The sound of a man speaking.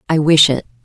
No: female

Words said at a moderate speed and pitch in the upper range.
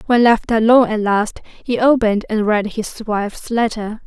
Yes: average, 175 wpm; high, 220 Hz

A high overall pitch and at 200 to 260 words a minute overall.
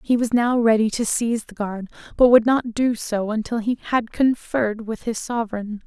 Yes: high, 225 Hz; fast, 205 wpm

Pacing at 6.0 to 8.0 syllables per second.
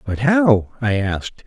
No: 3.9 syllables/s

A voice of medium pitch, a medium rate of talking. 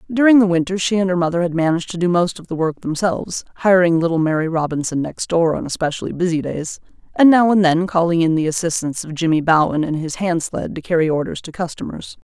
No: medium, 170 Hz; fast, 225 wpm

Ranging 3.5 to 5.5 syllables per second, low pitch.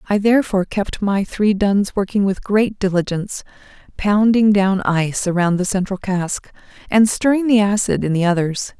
No: 5.0 syllables/s; high, 200 Hz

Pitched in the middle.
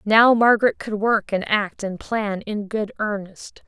No: high, 210 Hz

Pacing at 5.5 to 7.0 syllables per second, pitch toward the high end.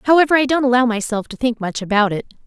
Yes: 6.7 syllables/s; high, 240 Hz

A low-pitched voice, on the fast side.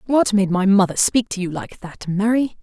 No: high, 205 Hz; fast, 230 wpm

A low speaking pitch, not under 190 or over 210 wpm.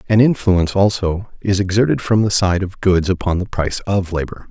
Yes: very low, 95 Hz; average, 200 wpm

